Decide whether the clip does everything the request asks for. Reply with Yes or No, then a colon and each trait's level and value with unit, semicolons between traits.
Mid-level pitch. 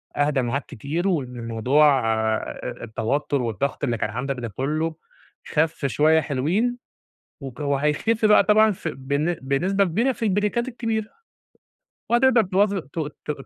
Yes: medium, 150 Hz